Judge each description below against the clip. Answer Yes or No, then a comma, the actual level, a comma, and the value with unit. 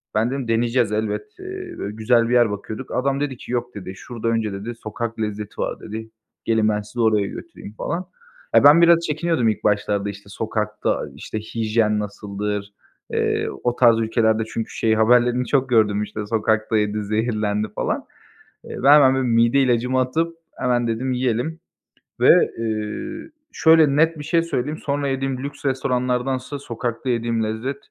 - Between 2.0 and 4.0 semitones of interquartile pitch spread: Yes, average, 3.6 semitones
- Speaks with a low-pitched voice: Yes, low, 115 Hz